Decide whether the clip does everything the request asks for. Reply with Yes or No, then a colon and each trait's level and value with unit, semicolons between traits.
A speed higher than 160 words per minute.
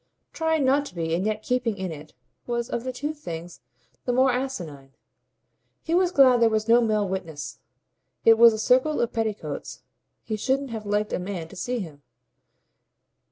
Yes: average, 180 wpm